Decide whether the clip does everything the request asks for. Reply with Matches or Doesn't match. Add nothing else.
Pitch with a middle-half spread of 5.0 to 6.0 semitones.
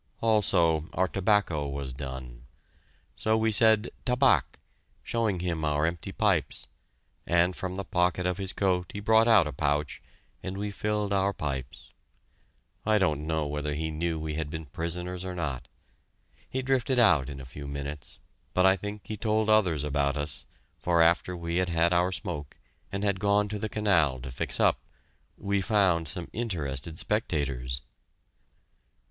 Matches